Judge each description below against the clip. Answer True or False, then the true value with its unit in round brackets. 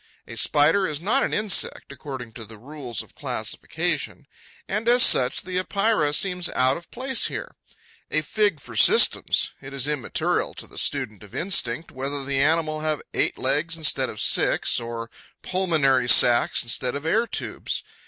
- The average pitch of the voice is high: False (150 Hz)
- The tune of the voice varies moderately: False (5.9 semitones)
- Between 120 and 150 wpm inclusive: False (165 wpm)